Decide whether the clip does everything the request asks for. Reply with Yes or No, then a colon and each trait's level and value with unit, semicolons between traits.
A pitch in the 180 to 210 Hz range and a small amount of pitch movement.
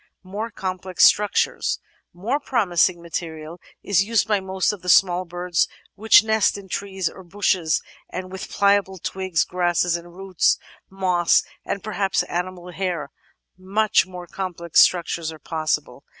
Yes: medium, 185 Hz; narrow, 2.1 semitones